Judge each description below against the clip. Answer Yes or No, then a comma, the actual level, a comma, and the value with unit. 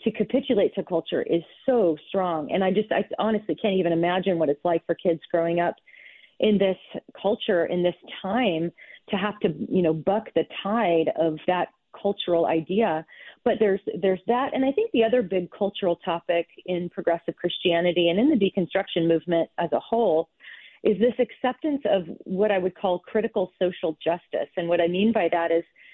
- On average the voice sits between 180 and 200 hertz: Yes, medium, 185 Hz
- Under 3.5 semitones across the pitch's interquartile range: No, average, 4.1 semitones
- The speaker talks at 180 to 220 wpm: Yes, average, 185 wpm